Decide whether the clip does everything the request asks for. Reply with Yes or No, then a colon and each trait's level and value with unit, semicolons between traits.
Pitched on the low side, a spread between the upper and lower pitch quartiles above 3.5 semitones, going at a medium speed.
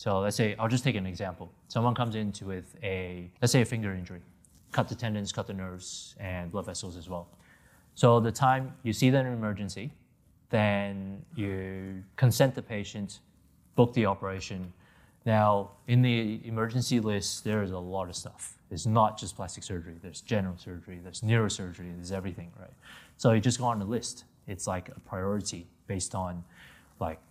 Yes: low, 100 Hz; average, 3.9 semitones; average, 185 wpm